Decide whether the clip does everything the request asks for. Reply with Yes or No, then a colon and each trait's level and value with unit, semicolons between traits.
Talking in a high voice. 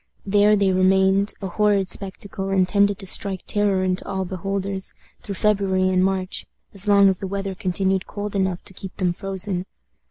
Yes: high, 195 Hz